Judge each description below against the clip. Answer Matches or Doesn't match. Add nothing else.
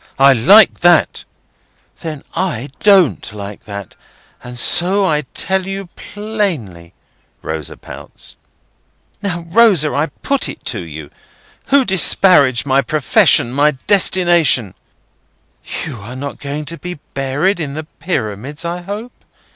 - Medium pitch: Matches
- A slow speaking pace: Matches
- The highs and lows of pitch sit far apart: Matches